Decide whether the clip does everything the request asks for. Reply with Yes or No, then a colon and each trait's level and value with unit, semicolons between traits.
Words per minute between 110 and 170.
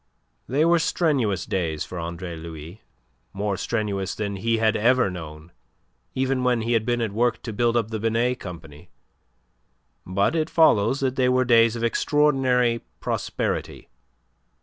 Yes: average, 150 wpm